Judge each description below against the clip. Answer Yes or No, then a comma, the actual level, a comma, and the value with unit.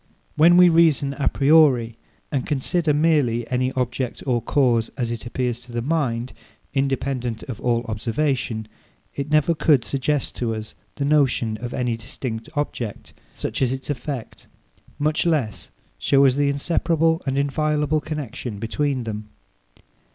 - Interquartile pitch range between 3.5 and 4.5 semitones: Yes, average, 3.9 semitones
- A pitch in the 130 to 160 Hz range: Yes, low, 135 Hz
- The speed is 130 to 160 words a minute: Yes, average, 145 wpm